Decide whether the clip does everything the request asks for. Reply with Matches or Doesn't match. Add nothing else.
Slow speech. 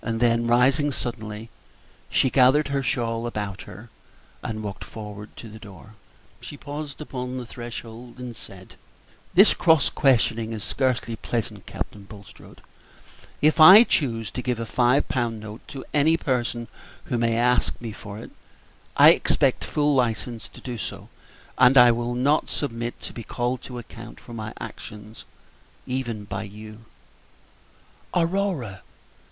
Doesn't match